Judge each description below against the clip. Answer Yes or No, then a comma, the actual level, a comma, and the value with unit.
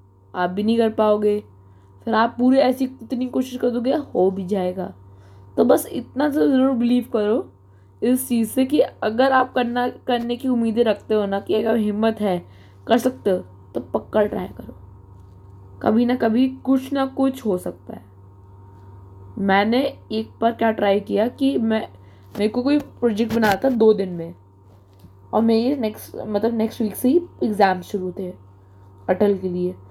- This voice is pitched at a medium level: No, high, 210 Hz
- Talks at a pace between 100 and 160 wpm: No, average, 175 wpm